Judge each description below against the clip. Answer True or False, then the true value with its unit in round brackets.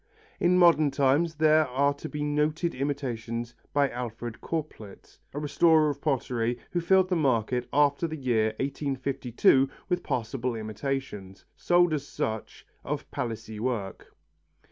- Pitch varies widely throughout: False (4.5 semitones)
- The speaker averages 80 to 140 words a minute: True (135 wpm)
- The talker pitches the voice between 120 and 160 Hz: True (140 Hz)